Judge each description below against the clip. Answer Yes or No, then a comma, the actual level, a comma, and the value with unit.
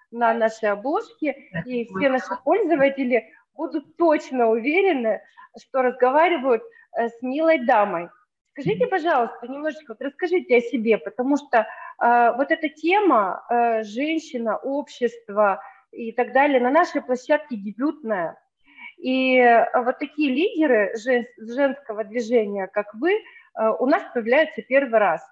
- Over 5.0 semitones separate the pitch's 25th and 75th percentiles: Yes, wide, 5.4 semitones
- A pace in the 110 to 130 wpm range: Yes, average, 125 wpm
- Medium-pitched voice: No, very high, 260 Hz